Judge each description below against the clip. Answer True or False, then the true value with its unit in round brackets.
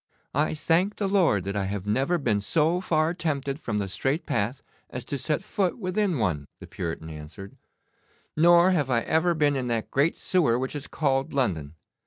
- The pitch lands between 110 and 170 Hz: True (140 Hz)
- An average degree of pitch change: False (8.1 semitones)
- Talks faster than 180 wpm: True (190 wpm)